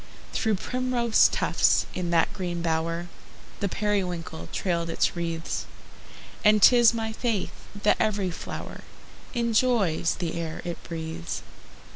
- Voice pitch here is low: No, medium, 185 Hz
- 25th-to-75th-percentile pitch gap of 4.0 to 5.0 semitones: Yes, average, 4.7 semitones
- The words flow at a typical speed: No, slow, 120 wpm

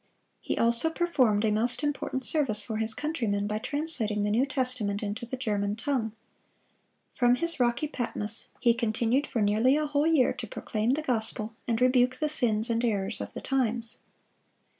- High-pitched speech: Yes, high, 235 Hz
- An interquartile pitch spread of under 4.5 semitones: Yes, average, 3.7 semitones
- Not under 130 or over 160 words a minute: No, average, 175 wpm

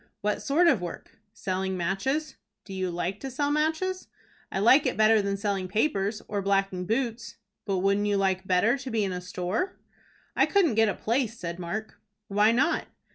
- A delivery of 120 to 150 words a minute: No, average, 185 wpm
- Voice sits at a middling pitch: No, high, 210 Hz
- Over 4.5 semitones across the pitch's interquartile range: Yes, average, 4.9 semitones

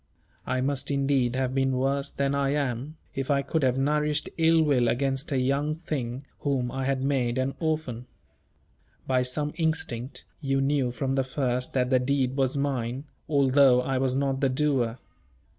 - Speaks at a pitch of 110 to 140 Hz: Yes, low, 135 Hz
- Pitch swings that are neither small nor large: No, narrow, 1.8 semitones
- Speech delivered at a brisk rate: No, average, 175 wpm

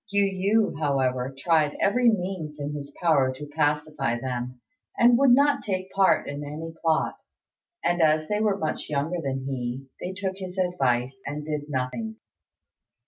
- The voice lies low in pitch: No, medium, 155 Hz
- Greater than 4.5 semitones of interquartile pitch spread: Yes, wide, 5.5 semitones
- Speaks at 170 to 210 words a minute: No, average, 160 wpm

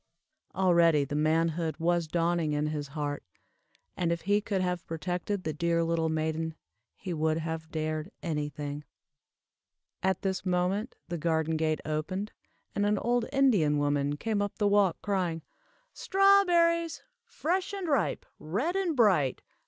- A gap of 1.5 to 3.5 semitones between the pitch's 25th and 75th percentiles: No, average, 4.5 semitones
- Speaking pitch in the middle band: Yes, medium, 170 Hz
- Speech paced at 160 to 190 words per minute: No, average, 145 wpm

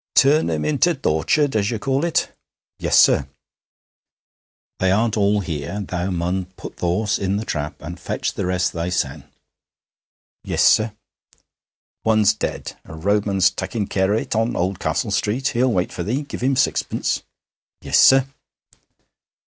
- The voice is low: Yes, low, 100 Hz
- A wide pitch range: No, average, 4.6 semitones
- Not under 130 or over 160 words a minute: Yes, average, 155 wpm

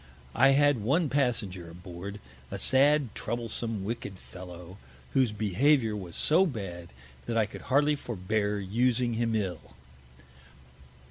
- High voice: No, low, 110 Hz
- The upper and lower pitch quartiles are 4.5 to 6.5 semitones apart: Yes, average, 5.3 semitones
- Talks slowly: Yes, slow, 125 wpm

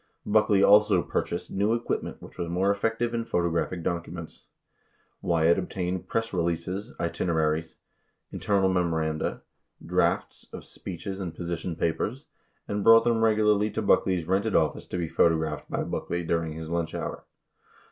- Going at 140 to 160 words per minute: Yes, average, 155 wpm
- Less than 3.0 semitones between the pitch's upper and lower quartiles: No, average, 3.7 semitones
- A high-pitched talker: No, very low, 90 Hz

